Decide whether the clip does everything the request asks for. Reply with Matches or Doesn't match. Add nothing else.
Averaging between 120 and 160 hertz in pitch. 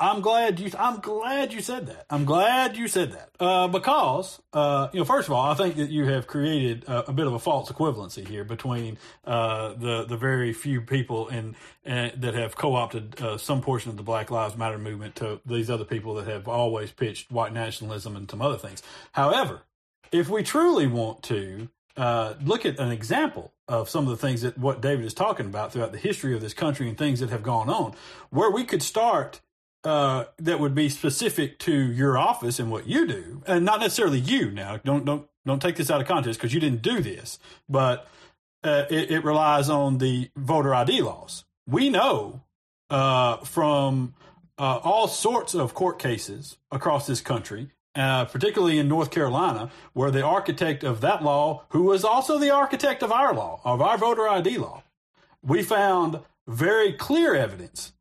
Matches